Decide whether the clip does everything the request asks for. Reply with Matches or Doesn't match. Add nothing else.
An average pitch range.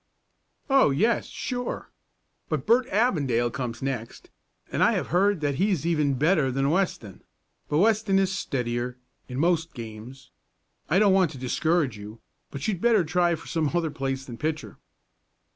Doesn't match